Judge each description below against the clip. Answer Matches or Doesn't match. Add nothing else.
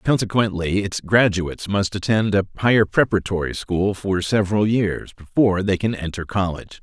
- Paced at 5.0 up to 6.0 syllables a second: Matches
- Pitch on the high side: Doesn't match